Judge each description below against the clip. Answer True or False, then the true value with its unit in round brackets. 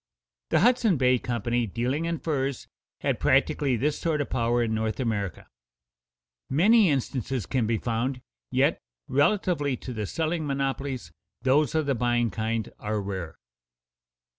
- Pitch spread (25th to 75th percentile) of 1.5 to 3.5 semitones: False (4.2 semitones)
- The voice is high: False (130 Hz)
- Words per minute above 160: False (140 wpm)